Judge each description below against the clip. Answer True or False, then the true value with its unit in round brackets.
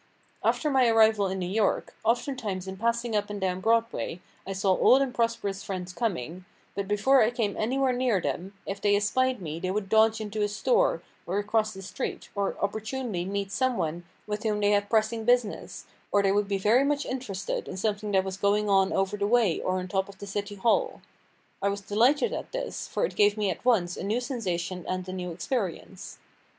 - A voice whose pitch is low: False (205 Hz)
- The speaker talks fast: True (210 wpm)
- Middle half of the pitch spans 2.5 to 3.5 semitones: True (3.2 semitones)